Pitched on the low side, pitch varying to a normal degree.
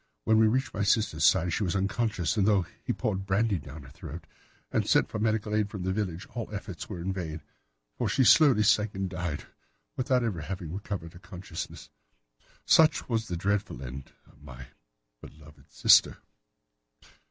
Yes: very low, 95 Hz; average, 4.0 semitones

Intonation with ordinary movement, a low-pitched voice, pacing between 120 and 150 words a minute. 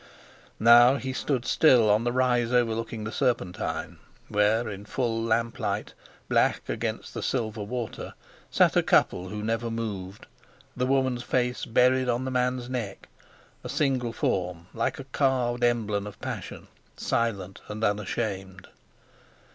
Yes: average, 3.0 semitones; low, 115 Hz; average, 140 wpm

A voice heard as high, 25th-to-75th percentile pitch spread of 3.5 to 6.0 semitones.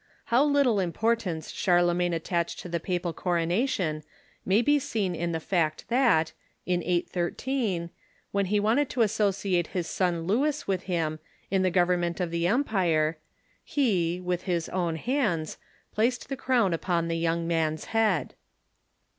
No: medium, 180 Hz; average, 4.6 semitones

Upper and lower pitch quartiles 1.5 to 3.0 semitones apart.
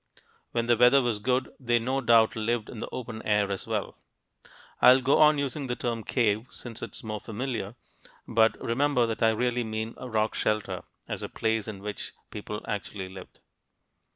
Yes: narrow, 2.4 semitones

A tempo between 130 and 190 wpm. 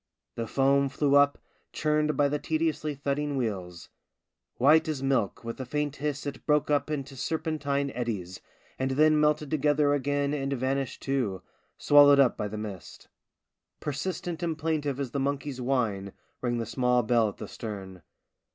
Yes: average, 160 wpm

